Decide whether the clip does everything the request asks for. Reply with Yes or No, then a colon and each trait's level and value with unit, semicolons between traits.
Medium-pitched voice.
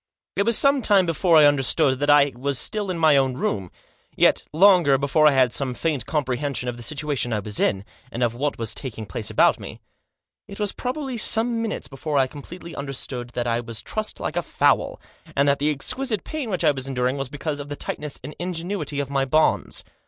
Yes: medium, 145 Hz